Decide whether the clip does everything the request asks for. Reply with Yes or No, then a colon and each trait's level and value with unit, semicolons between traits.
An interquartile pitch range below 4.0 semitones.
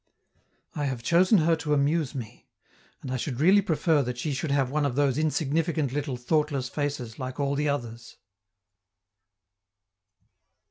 Yes: average, 3.1 semitones